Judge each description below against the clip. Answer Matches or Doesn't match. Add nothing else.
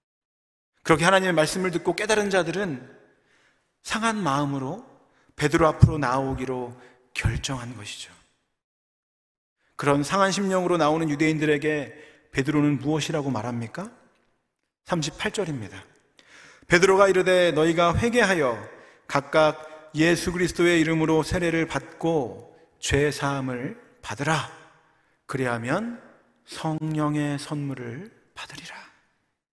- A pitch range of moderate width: Matches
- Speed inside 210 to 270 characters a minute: Matches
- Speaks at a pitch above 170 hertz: Doesn't match